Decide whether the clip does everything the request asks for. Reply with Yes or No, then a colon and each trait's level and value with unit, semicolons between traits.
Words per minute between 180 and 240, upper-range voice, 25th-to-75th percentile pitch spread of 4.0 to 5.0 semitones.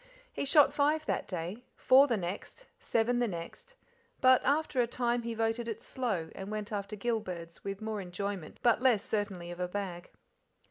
Yes: average, 185 wpm; high, 220 Hz; average, 4.4 semitones